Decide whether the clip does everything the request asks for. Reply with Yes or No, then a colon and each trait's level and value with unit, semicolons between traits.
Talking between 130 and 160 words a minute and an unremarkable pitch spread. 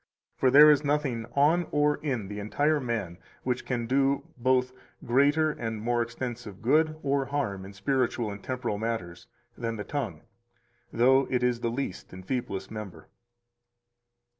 Yes: average, 155 wpm; average, 4.4 semitones